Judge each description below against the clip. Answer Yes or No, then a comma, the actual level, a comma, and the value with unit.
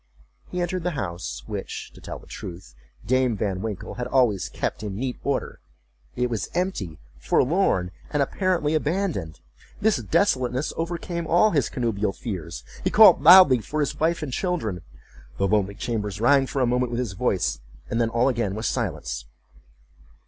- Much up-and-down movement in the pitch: Yes, wide, 7.6 semitones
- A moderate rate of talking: Yes, average, 160 wpm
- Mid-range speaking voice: No, low, 125 Hz